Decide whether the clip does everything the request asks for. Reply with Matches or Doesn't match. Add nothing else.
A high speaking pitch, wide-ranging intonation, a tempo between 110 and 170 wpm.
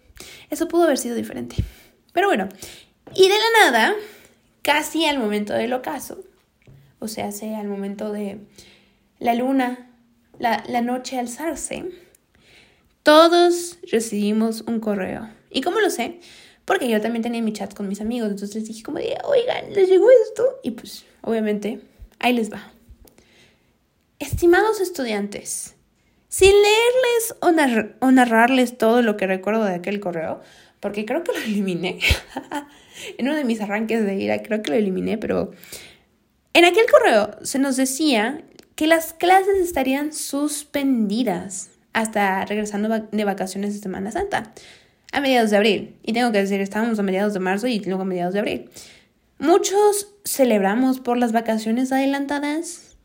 Matches